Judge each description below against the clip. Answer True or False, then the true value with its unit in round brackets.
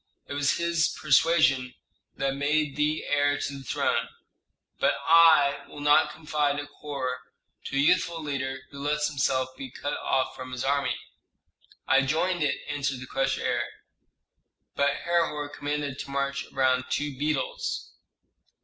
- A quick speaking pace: False (150 wpm)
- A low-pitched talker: False (145 Hz)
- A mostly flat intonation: True (1.8 semitones)